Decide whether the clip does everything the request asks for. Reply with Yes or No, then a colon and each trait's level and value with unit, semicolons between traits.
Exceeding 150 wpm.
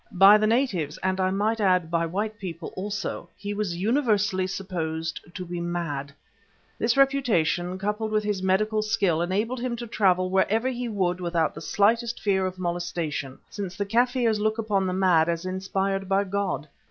Yes: average, 175 wpm